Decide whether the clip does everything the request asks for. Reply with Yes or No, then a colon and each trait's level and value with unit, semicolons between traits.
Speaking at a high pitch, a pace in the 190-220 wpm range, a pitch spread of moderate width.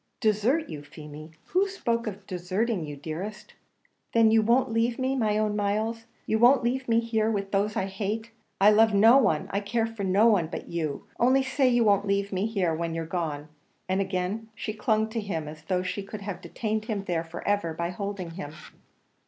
Yes: high, 205 Hz; fast, 205 wpm; average, 3.9 semitones